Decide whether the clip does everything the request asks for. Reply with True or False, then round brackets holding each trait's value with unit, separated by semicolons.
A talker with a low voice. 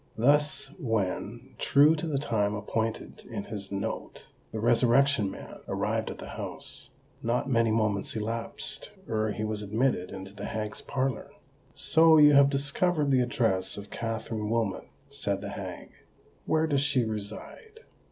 True (115 Hz)